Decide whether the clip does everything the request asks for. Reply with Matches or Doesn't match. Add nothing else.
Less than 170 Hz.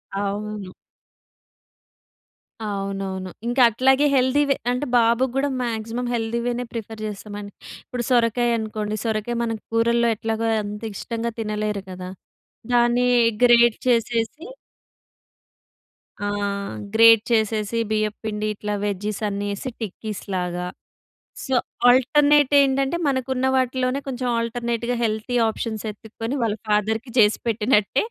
Doesn't match